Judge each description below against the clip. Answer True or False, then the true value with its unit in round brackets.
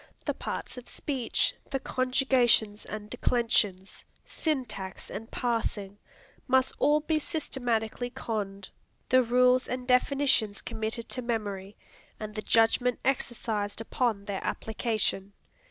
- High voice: True (235 Hz)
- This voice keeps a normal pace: False (115 wpm)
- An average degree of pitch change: True (3.4 semitones)